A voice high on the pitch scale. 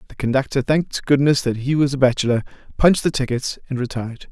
No: low, 135 Hz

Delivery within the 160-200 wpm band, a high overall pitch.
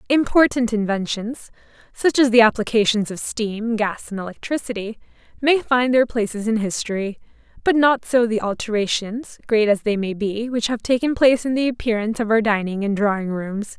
Yes: average, 175 wpm; high, 225 Hz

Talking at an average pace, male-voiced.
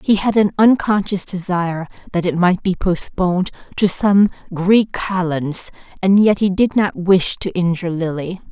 No: average, 160 wpm; female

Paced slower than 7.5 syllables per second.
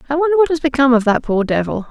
No: 7.6 syllables/s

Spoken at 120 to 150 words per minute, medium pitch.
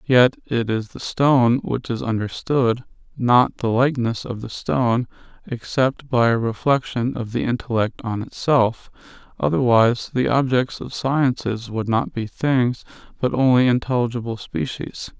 No: average, 140 wpm; low, 120 Hz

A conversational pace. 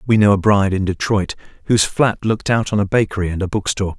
No: fast, 240 wpm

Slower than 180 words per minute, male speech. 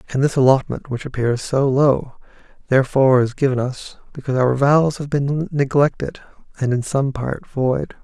Yes: average, 165 wpm; male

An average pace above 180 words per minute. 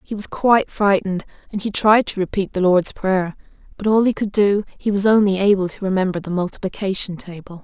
Yes: fast, 205 wpm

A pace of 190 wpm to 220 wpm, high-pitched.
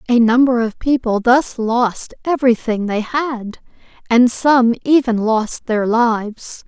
No: slow, 135 wpm; high, 235 Hz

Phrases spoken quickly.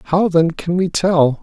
Yes: fast, 210 wpm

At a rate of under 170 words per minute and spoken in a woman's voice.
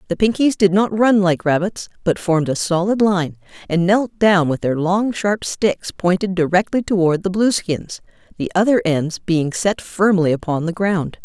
No: average, 180 wpm; female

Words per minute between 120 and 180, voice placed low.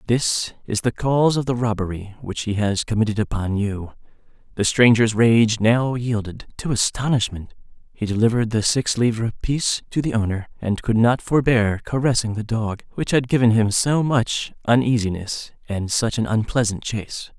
Yes: average, 165 wpm; low, 115 Hz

